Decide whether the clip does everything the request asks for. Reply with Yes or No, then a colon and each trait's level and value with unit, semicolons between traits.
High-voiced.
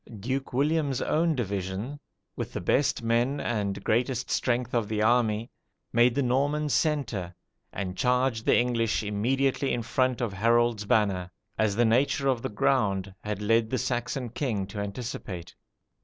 No: low, 120 Hz